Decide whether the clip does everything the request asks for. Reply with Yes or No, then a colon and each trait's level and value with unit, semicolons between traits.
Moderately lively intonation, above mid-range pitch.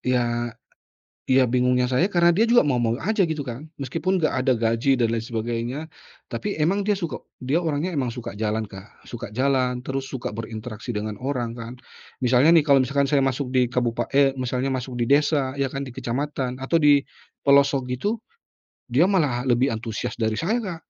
No: average, 3.4 semitones; low, 130 Hz